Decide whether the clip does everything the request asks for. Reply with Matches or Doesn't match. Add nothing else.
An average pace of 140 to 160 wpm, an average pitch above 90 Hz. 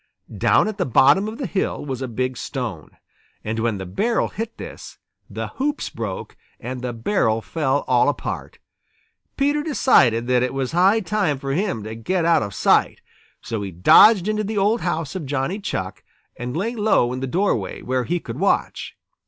Doesn't match